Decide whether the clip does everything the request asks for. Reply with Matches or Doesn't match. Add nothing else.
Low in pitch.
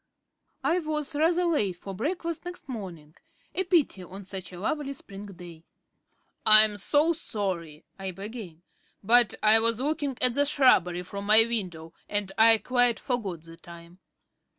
Doesn't match